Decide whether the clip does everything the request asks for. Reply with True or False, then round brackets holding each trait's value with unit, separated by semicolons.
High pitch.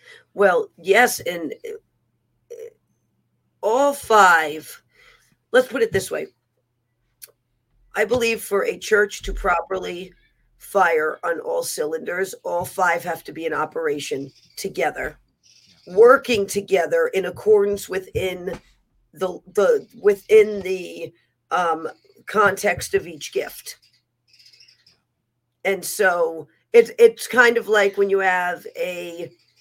True (200 Hz)